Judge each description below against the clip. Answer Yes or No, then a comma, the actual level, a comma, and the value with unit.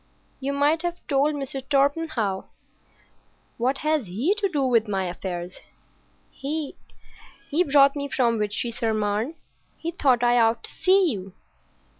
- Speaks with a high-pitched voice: Yes, very high, 270 Hz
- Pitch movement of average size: Yes, average, 5.0 semitones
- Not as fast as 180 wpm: Yes, average, 140 wpm